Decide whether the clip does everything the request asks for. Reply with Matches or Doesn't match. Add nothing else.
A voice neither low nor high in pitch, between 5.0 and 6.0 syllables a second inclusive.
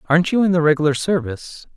Doesn't match